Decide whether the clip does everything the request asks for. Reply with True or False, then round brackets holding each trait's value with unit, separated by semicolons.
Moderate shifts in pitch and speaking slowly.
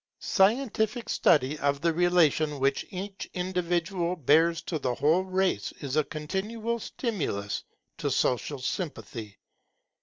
True (4.9 semitones; 120 wpm)